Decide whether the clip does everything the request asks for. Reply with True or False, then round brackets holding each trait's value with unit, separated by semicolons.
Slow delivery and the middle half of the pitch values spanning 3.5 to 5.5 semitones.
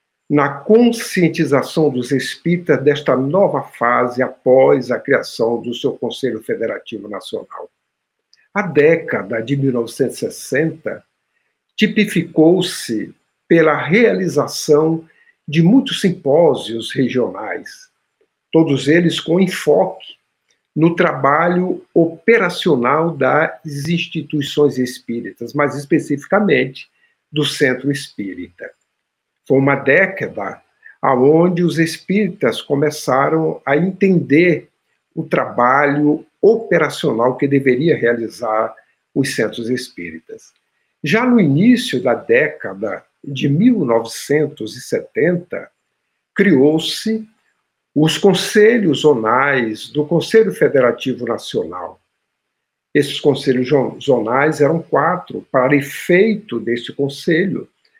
True (85 wpm; 5.1 semitones)